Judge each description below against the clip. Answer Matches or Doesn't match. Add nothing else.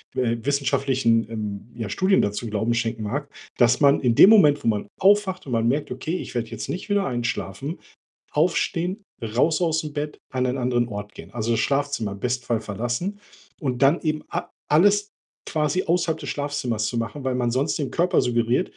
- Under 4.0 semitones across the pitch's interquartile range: Doesn't match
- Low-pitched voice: Matches